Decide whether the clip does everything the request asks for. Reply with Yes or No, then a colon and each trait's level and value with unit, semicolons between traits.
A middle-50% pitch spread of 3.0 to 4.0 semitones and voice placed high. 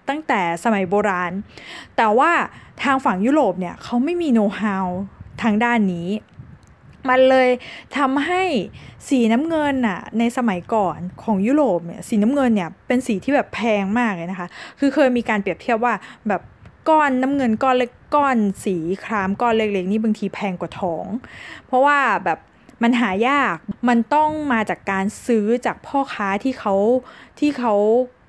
No: average, 4.8 semitones; high, 230 Hz